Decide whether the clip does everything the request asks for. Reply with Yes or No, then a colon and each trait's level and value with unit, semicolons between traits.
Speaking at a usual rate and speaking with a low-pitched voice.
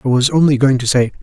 No: fast, 295 wpm; low, 130 Hz